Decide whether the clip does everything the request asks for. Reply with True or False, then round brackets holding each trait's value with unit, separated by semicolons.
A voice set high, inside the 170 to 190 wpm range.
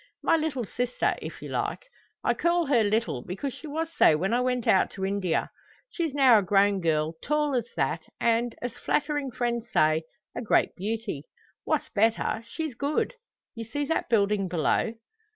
True (230 Hz; 175 wpm)